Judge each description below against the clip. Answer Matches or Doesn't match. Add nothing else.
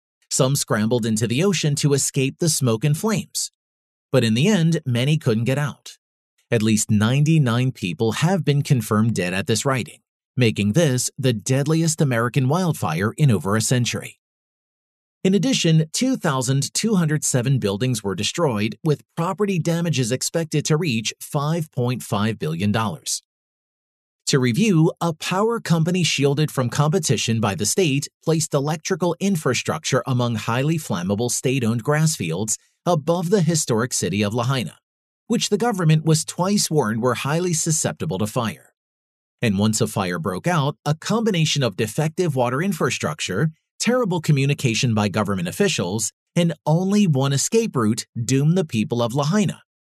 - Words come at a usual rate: Matches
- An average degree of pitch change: Doesn't match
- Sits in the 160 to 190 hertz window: Doesn't match